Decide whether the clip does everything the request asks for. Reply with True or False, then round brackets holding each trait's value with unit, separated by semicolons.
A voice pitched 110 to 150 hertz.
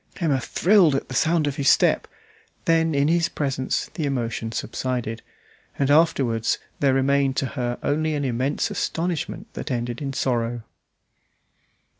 True (140 Hz)